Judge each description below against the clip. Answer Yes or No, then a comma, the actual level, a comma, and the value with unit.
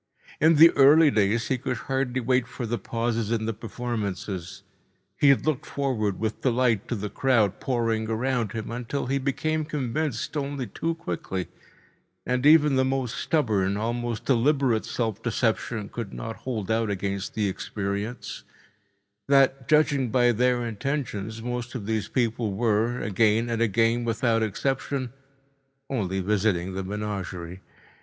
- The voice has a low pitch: Yes, low, 115 Hz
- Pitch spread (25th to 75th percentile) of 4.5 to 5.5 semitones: No, average, 3.8 semitones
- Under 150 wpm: Yes, average, 140 wpm